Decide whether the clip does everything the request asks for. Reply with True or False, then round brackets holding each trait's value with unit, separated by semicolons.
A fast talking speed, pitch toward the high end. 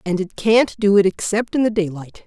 True (240 wpm; 205 Hz)